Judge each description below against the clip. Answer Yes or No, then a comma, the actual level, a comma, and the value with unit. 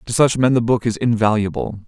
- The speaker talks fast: Yes, fast, 225 wpm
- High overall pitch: No, low, 115 Hz